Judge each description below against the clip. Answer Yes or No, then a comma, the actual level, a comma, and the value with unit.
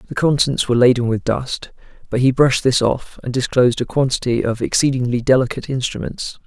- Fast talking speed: No, average, 175 wpm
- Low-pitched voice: Yes, low, 125 Hz